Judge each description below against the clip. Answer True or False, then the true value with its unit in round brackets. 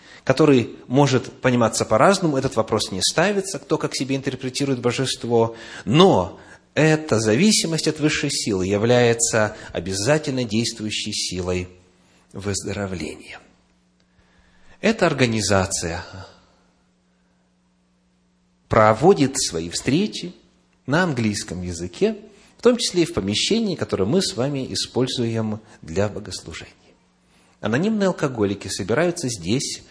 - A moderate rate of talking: False (100 wpm)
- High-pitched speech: False (115 Hz)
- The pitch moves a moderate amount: False (7.3 semitones)